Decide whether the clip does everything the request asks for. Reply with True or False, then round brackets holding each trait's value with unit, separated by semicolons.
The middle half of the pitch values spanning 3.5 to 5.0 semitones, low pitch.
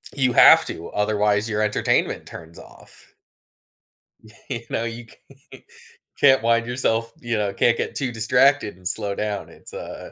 False (2.5 semitones; 115 Hz)